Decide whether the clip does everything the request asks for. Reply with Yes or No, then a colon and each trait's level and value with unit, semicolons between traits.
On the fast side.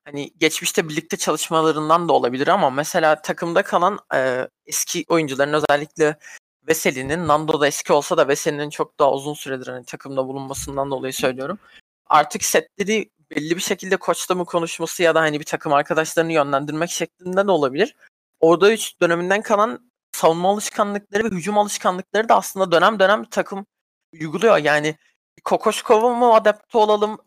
Yes: fast, 150 wpm